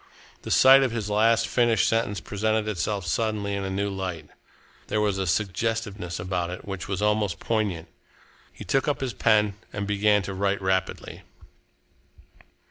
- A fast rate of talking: No, average, 160 wpm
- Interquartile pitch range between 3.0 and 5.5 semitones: No, narrow, 2.4 semitones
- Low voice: Yes, low, 100 Hz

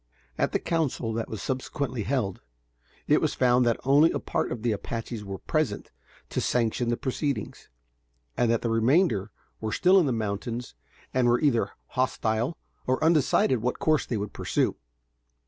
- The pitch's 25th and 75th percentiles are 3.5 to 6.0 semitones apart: No, average, 3.1 semitones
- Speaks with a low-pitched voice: Yes, low, 120 Hz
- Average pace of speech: Yes, average, 165 wpm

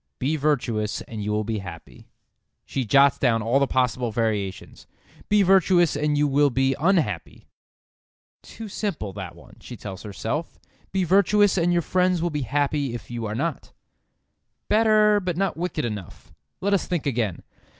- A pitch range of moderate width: No, wide, 7.8 semitones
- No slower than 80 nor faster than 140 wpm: No, average, 165 wpm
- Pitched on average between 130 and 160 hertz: Yes, medium, 140 Hz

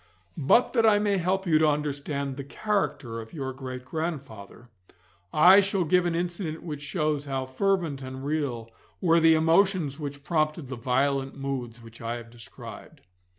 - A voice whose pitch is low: No, medium, 145 Hz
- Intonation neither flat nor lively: Yes, average, 4.5 semitones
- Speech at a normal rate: Yes, average, 165 wpm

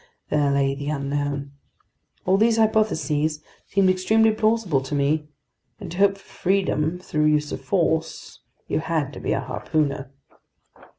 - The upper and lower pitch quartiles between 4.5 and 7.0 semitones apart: Yes, average, 5.3 semitones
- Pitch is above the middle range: No, medium, 155 Hz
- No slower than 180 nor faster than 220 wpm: No, average, 145 wpm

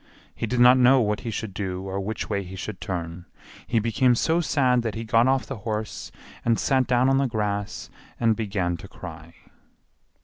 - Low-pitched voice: Yes, low, 110 Hz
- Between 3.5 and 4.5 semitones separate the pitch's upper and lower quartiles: Yes, average, 4.2 semitones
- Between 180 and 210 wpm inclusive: Yes, average, 200 wpm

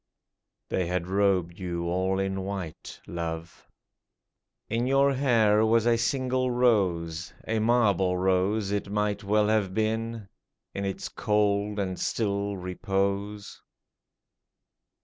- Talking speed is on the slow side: Yes, slow, 120 wpm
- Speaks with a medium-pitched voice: No, low, 100 Hz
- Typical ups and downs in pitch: Yes, average, 3.0 semitones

